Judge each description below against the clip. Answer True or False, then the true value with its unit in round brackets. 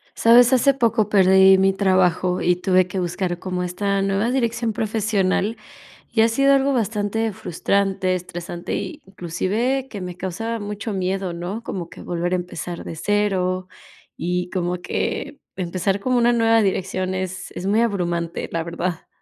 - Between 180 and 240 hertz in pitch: True (190 Hz)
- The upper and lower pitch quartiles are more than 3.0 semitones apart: True (3.6 semitones)